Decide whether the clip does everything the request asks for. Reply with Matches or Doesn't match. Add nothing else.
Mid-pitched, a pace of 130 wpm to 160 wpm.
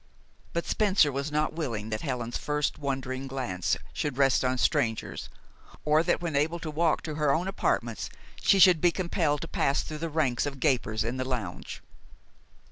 Doesn't match